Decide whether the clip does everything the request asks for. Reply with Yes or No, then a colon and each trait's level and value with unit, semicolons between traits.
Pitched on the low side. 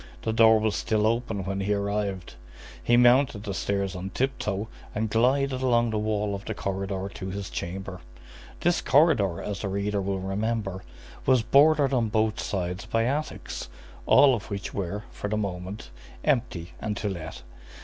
Yes: low, 105 Hz